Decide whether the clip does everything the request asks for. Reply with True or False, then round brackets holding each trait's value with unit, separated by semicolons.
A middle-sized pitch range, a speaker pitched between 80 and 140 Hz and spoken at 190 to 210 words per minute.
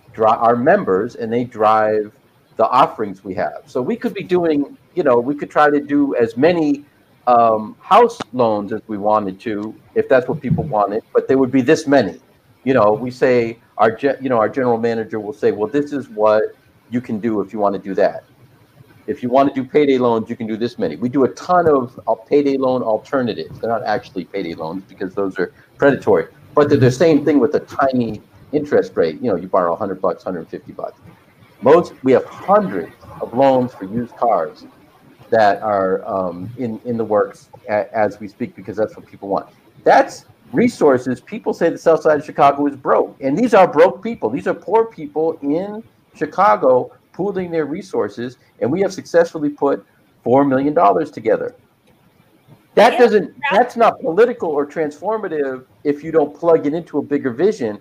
False (5.7 semitones; 135 Hz; 195 wpm)